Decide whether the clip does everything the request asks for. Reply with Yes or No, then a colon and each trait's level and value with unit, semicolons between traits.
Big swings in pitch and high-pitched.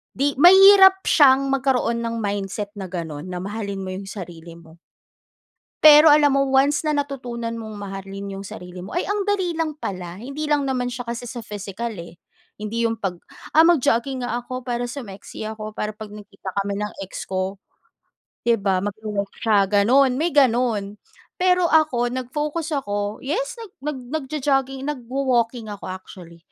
Yes: wide, 5.8 semitones; high, 235 Hz